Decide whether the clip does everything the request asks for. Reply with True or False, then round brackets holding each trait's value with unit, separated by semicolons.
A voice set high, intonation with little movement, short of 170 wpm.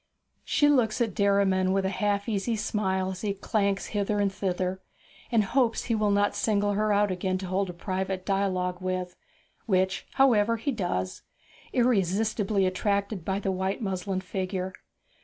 True (195 Hz; 2.1 semitones; 160 wpm)